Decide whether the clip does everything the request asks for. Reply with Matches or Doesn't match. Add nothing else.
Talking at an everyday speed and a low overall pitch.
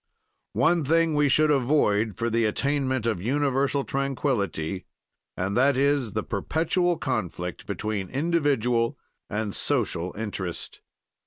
Doesn't match